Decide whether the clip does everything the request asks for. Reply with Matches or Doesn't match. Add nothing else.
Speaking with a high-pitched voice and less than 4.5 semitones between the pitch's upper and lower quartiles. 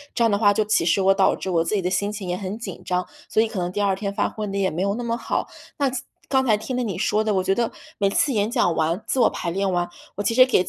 Matches